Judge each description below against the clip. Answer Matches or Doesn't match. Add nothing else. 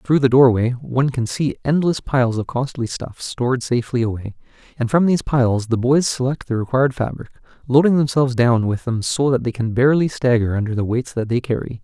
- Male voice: Matches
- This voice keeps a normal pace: Doesn't match